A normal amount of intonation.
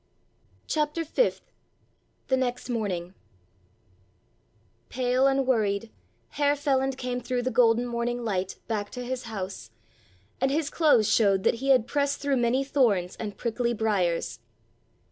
Yes: average, 3.6 semitones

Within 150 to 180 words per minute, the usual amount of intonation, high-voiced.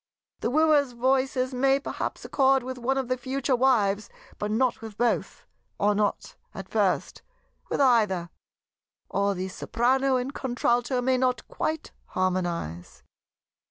No: slow, 135 wpm; average, 4.1 semitones; very high, 250 Hz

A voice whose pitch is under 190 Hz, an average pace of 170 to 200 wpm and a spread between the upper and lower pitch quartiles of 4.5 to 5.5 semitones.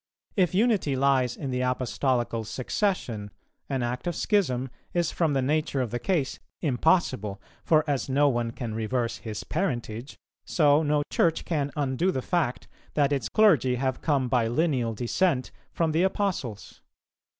No: low, 135 Hz; average, 155 wpm; average, 4.8 semitones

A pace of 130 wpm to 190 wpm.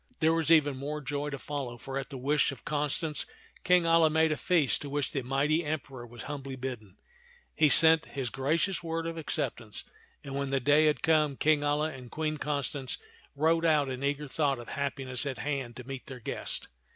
No: average, 200 wpm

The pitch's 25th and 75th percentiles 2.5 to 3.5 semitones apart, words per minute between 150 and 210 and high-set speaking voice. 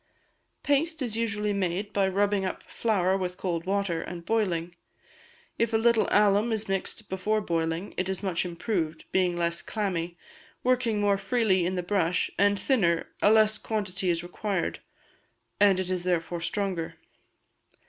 Yes: average, 3.2 semitones; average, 155 wpm; high, 195 Hz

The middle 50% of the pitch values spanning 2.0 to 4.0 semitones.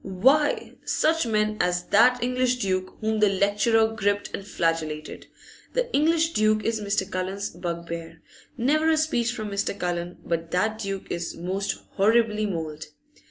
No: average, 4.7 semitones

